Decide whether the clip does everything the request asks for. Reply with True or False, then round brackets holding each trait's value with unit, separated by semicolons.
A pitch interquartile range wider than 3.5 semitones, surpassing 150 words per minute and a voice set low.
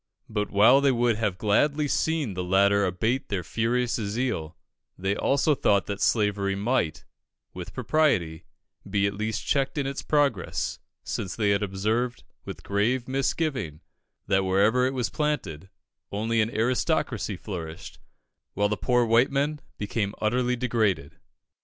False (4.4 semitones; 145 wpm; 110 Hz)